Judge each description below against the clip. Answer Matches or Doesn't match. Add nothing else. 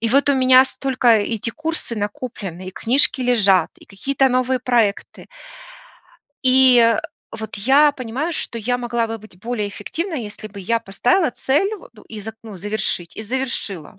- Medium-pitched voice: Doesn't match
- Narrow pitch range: Doesn't match